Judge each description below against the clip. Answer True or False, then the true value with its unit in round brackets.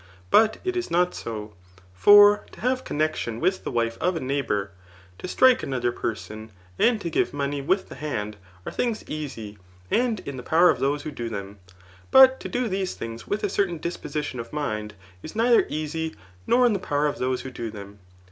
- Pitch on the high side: False (150 Hz)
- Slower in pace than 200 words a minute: False (205 wpm)